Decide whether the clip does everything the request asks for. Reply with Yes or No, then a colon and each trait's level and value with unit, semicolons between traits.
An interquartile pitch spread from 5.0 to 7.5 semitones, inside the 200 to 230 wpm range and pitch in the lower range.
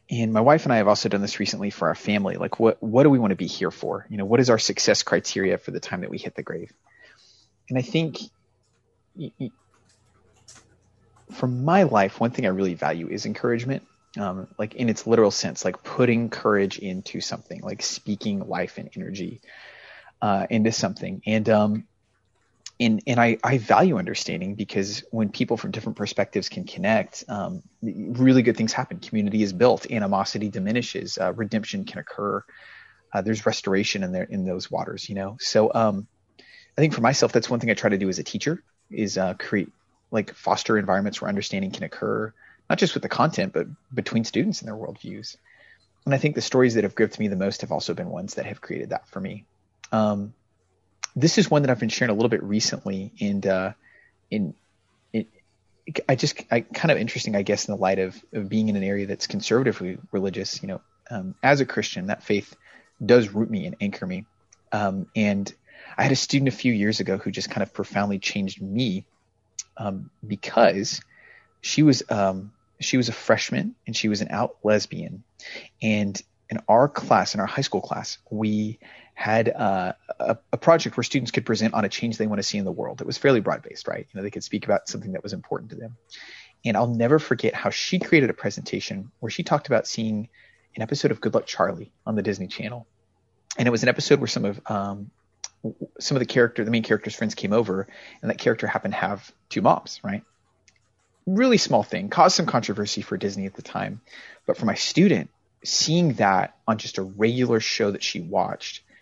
No: average, 3.8 semitones; fast, 205 wpm; low, 110 Hz